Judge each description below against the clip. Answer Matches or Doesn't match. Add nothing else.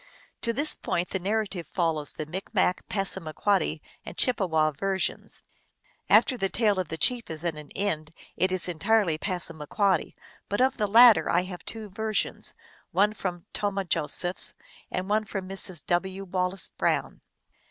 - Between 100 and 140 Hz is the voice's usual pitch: Doesn't match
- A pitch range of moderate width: Matches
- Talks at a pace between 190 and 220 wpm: Doesn't match